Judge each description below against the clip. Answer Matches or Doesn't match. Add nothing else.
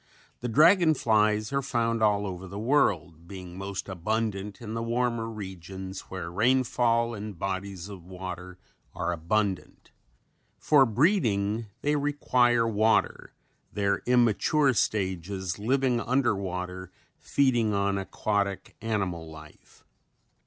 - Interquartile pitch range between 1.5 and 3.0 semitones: Doesn't match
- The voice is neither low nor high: Doesn't match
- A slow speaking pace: Matches